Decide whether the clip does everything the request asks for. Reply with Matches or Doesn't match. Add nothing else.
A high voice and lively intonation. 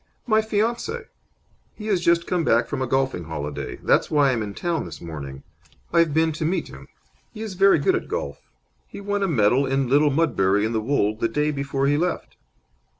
Doesn't match